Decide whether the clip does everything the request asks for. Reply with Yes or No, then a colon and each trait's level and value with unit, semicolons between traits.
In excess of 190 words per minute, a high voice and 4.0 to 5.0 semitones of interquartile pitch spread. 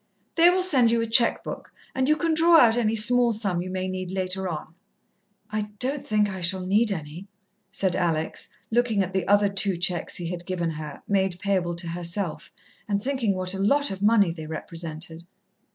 Yes: average, 200 wpm; high, 195 Hz; average, 4.4 semitones